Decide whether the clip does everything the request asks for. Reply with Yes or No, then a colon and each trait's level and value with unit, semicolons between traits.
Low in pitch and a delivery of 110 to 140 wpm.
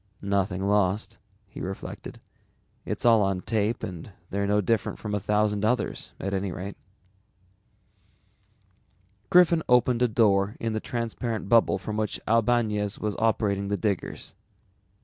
Yes: low, 105 Hz; slow, 135 wpm